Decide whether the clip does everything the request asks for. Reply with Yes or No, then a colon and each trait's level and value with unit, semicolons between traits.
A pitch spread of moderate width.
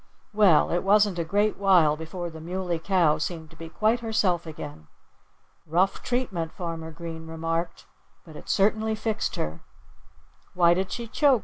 Yes: average, 4.1 semitones